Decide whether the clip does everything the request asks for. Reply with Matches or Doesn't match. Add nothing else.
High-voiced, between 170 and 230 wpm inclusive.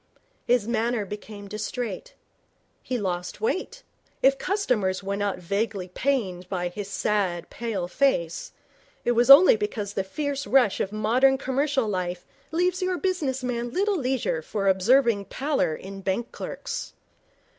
Doesn't match